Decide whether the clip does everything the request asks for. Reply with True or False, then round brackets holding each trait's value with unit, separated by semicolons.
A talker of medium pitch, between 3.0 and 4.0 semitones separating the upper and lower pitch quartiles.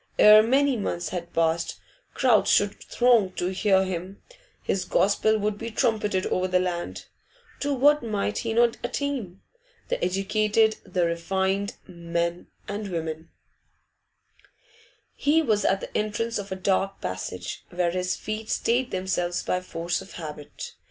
False (195 Hz; 3.6 semitones)